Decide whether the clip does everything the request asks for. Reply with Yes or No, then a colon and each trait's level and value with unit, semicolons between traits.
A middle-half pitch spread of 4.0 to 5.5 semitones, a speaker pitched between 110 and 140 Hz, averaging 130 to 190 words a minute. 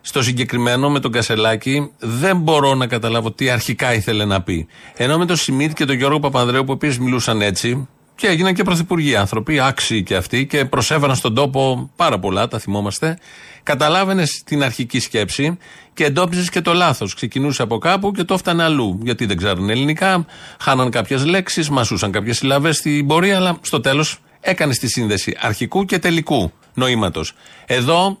Yes: average, 5.2 semitones; low, 135 Hz; fast, 170 wpm